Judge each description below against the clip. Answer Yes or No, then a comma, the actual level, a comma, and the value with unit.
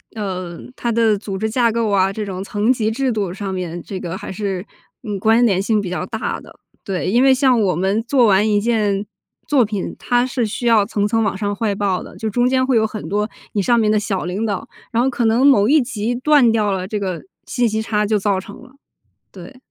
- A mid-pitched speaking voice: No, high, 215 Hz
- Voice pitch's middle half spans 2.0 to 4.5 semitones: Yes, average, 3.1 semitones